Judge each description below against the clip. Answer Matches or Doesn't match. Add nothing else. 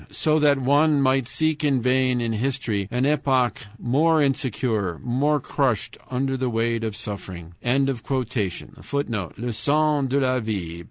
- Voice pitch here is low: Matches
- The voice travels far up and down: Doesn't match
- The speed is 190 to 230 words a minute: Doesn't match